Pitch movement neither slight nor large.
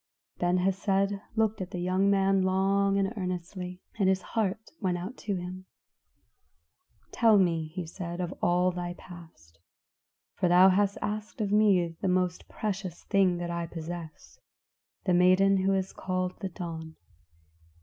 No: narrow, 1.9 semitones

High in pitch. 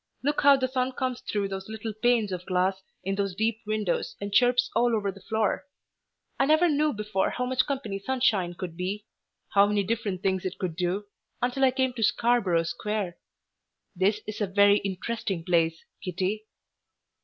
Yes: high, 210 Hz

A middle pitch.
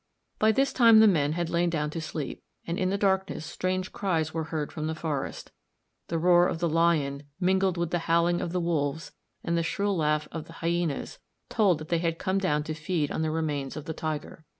Yes: medium, 165 Hz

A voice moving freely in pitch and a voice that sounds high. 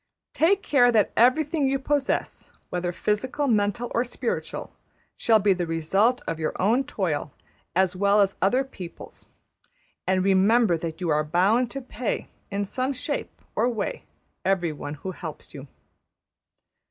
Yes: wide, 5.9 semitones; high, 205 Hz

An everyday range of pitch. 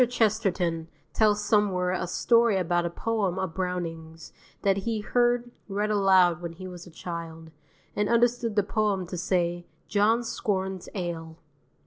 Yes: average, 3.4 semitones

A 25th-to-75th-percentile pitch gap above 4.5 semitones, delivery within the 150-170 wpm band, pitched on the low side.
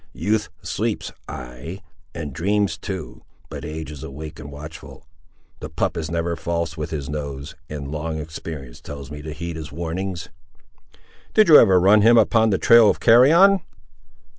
Yes: average, 4.9 semitones; average, 165 wpm; very low, 80 Hz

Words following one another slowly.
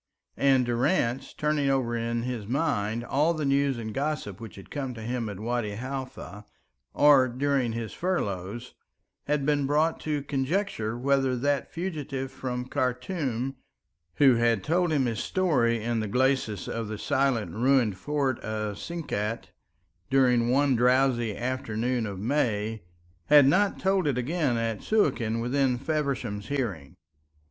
No: average, 145 wpm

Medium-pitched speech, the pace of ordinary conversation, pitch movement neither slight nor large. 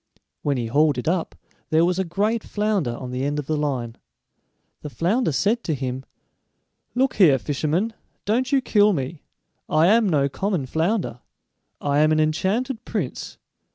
No: medium, 160 Hz; average, 165 wpm; wide, 6.8 semitones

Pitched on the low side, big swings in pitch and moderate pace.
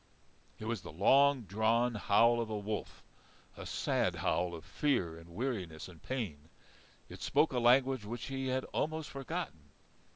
Yes: low, 115 Hz; wide, 6.4 semitones; average, 160 wpm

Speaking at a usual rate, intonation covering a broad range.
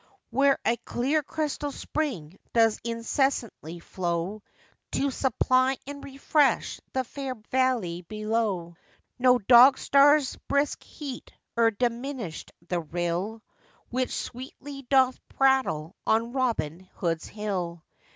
No: slow, 110 wpm; wide, 6.1 semitones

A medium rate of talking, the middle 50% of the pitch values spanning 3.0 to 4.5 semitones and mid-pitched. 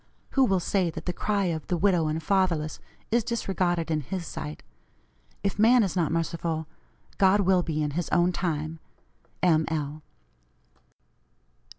Yes: average, 155 wpm; average, 3.3 semitones; medium, 175 Hz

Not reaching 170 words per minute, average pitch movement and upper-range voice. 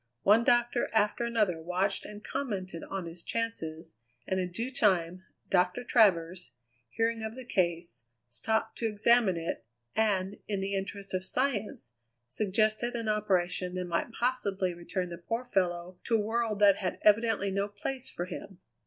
Yes: average, 160 wpm; average, 3.9 semitones; high, 200 Hz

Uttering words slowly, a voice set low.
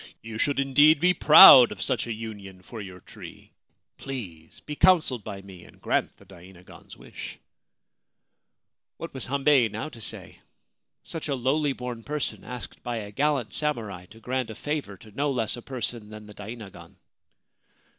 No: average, 170 wpm; low, 120 Hz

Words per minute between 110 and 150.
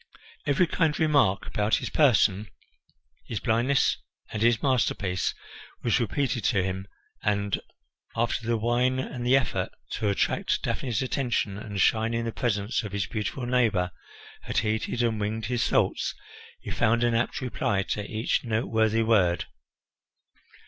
Yes: average, 145 wpm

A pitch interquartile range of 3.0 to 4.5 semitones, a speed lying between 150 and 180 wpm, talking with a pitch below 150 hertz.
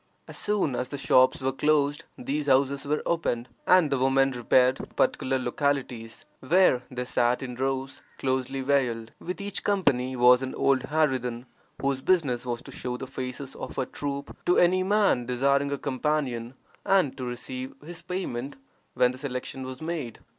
No: narrow, 2.6 semitones; average, 170 wpm; low, 135 Hz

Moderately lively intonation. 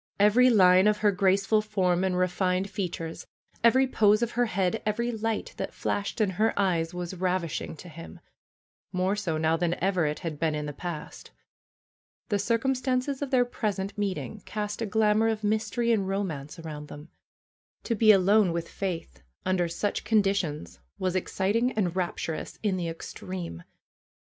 Yes: average, 3.7 semitones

